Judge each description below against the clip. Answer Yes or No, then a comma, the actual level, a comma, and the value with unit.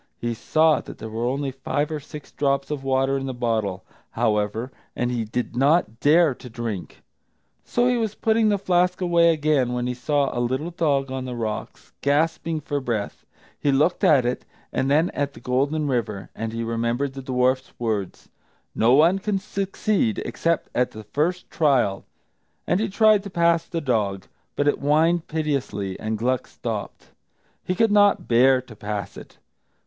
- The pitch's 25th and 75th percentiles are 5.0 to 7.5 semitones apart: Yes, wide, 5.5 semitones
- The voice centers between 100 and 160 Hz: Yes, low, 135 Hz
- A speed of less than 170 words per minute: No, average, 180 wpm